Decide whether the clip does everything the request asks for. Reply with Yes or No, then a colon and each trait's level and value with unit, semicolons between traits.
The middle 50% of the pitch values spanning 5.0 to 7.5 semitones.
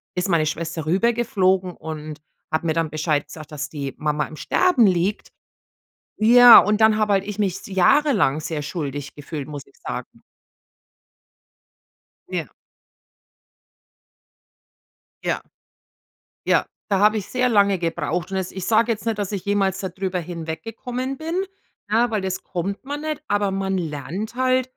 Yes: wide, 5.4 semitones